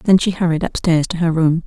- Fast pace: Yes, fast, 250 wpm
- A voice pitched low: No, medium, 170 Hz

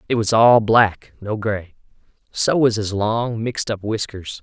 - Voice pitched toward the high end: No, low, 110 Hz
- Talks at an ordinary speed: Yes, average, 175 wpm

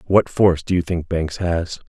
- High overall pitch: No, very low, 85 Hz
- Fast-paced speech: Yes, fast, 220 wpm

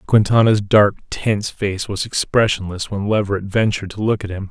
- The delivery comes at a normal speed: Yes, average, 175 wpm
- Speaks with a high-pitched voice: No, low, 100 Hz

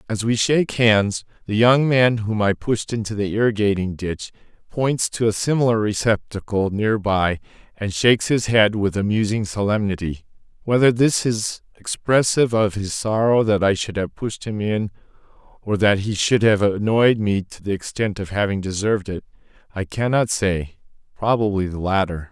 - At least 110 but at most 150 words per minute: No, average, 165 wpm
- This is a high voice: No, low, 105 Hz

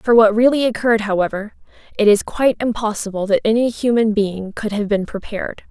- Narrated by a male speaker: No, female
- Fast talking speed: No, average, 180 wpm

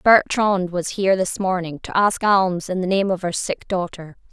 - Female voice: Yes, female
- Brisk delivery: Yes, fast, 210 wpm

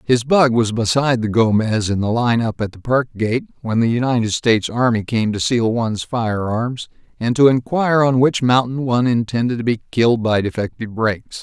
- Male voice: Yes, male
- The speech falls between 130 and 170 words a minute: No, average, 195 wpm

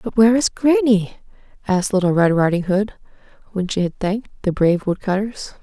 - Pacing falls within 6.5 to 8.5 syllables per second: No, 5.6 syllables/s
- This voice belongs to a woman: Yes, female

